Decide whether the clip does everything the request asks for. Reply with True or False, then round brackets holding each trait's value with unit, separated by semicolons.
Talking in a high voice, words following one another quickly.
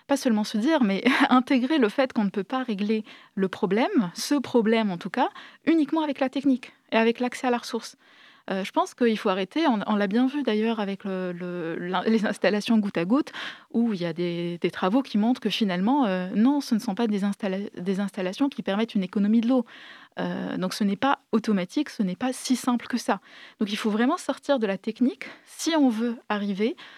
True (230 Hz; 225 wpm)